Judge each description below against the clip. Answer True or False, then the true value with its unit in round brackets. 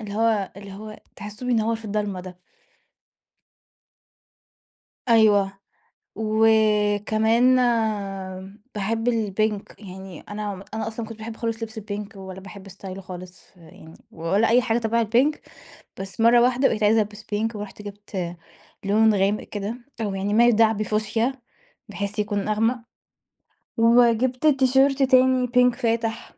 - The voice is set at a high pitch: True (215 Hz)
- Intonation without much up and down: True (2.2 semitones)